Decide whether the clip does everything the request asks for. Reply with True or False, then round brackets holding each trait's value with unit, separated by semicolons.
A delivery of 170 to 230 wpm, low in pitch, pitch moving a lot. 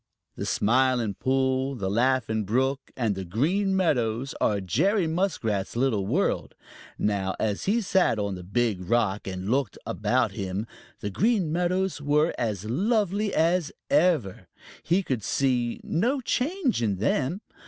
False (145 wpm; 130 Hz; 9.0 semitones)